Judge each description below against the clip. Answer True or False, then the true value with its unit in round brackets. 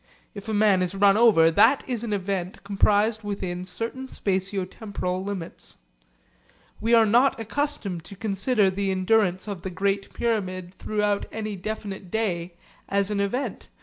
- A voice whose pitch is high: True (200 Hz)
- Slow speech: False (150 wpm)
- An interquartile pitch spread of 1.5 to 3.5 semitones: True (2.7 semitones)